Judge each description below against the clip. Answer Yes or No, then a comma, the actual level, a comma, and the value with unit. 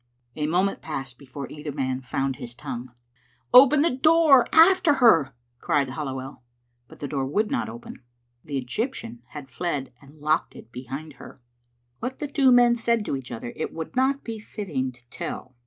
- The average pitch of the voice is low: No, medium, 150 Hz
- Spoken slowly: No, average, 175 wpm